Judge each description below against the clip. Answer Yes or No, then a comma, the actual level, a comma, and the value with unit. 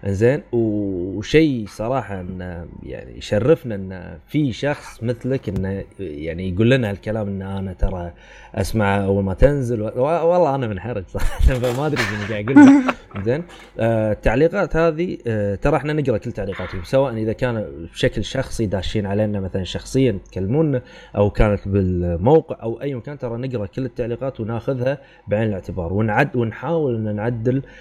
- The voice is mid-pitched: No, low, 110 Hz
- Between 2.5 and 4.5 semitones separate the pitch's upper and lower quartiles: No, average, 5.1 semitones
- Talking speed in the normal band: No, fast, 145 wpm